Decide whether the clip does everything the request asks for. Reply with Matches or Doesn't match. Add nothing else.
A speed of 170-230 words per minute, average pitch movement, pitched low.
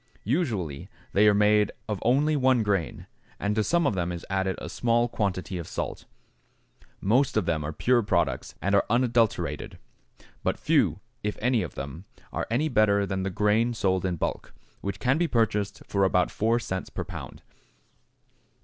Matches